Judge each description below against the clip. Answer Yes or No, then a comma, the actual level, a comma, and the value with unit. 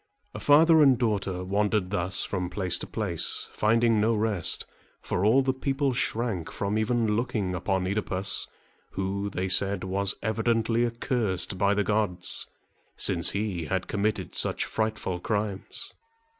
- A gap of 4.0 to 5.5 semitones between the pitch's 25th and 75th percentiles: No, average, 3.3 semitones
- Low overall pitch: Yes, low, 105 Hz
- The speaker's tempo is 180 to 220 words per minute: No, average, 140 wpm